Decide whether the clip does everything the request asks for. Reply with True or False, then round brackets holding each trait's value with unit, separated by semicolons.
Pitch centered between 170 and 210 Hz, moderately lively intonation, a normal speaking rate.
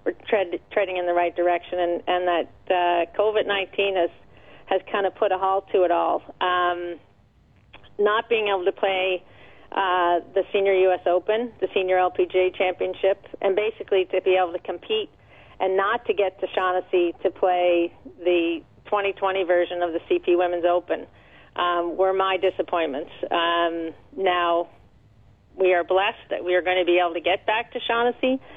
False (185 Hz; 2.0 semitones; 170 wpm)